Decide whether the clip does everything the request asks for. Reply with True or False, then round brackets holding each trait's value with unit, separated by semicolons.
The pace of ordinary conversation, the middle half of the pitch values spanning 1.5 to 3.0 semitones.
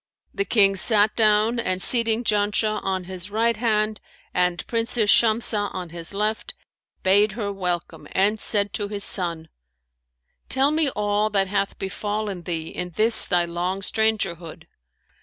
True (145 wpm; 2.7 semitones)